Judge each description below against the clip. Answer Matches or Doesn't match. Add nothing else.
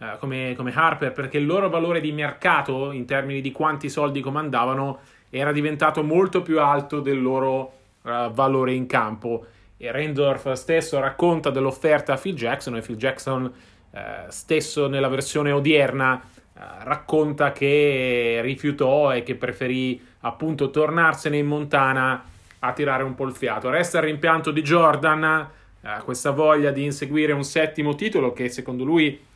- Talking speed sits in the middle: Matches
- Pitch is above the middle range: Doesn't match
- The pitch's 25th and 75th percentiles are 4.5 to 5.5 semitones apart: Doesn't match